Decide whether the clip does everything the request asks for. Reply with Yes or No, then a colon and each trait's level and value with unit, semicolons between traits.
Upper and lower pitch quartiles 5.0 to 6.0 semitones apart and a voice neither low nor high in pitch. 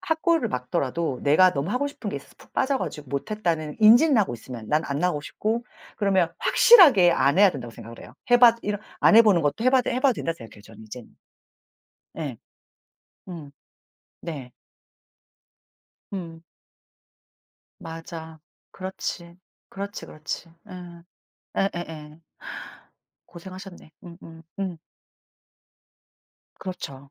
Yes: wide, 5.6 semitones; medium, 170 Hz